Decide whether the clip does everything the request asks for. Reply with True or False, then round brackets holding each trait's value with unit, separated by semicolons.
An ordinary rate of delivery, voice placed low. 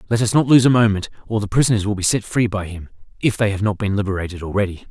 False (255 wpm; 105 Hz)